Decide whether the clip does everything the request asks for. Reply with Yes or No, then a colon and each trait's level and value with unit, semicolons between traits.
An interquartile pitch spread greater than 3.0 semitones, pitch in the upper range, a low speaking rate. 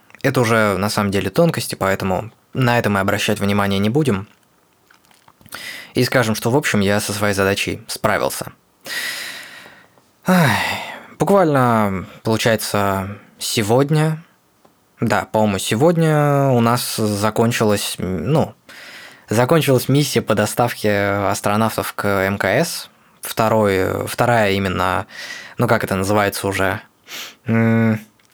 No: average, 3.5 semitones; low, 110 Hz; slow, 105 wpm